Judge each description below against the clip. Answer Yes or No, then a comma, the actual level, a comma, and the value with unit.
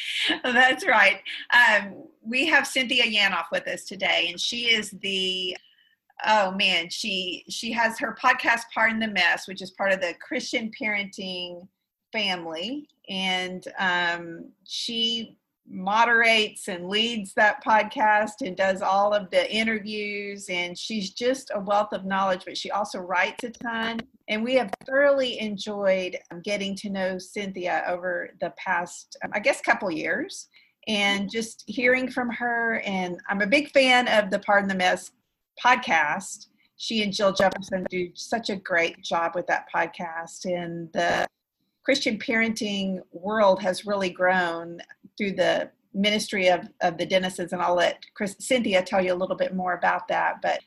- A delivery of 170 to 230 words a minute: No, average, 160 wpm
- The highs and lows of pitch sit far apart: No, average, 3.9 semitones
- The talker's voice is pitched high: Yes, high, 205 Hz